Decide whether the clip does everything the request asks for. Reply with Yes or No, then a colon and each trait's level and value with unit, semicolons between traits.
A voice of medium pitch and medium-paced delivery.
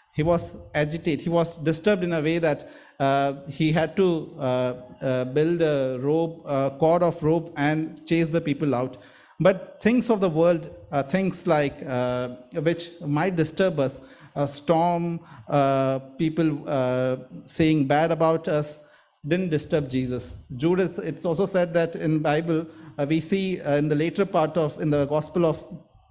Yes: medium, 155 Hz; average, 170 wpm